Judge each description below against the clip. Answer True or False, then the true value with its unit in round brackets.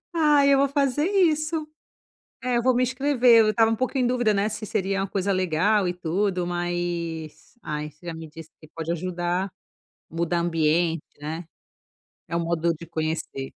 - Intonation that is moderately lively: False (6.7 semitones)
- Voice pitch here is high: False (180 Hz)